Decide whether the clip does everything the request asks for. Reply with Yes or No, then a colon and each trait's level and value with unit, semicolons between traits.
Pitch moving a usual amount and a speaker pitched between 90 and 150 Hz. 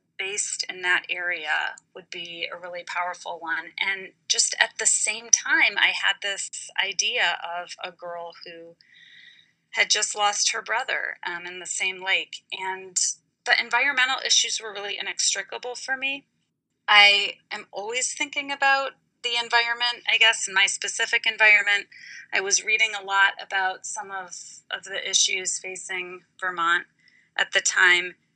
No: average, 4.6 semitones; high, 200 Hz